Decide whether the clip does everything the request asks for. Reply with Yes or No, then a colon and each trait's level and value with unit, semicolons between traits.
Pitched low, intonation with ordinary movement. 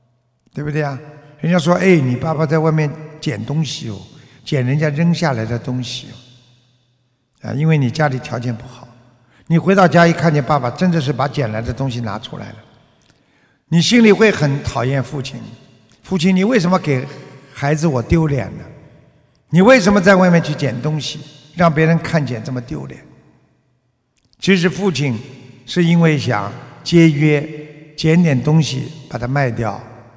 No: medium, 145 Hz; average, 4.3 semitones